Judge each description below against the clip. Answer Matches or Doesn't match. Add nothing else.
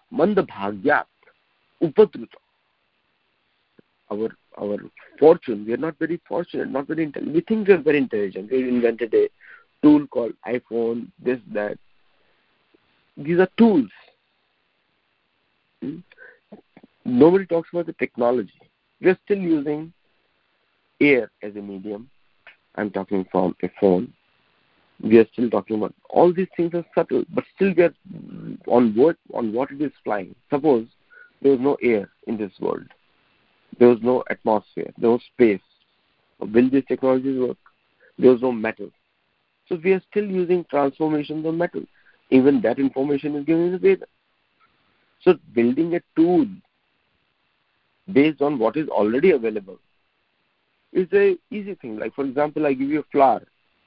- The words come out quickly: Doesn't match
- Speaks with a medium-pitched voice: Matches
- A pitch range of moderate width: Doesn't match